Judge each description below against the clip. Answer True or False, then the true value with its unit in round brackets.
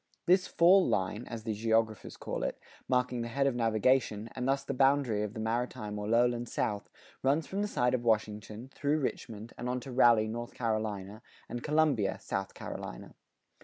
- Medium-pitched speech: False (120 Hz)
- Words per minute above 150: True (180 wpm)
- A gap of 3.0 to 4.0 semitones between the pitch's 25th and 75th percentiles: True (3.5 semitones)